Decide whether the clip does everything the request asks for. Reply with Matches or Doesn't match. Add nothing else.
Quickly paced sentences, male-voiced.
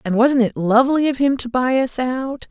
Doesn't match